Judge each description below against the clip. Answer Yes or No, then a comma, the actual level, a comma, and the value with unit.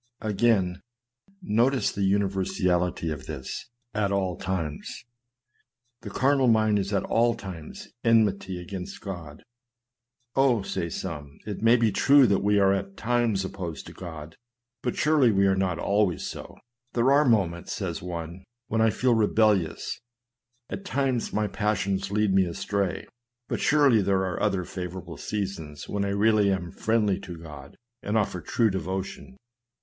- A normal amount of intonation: Yes, average, 3.7 semitones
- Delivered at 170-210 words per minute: No, average, 160 wpm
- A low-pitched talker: Yes, low, 100 Hz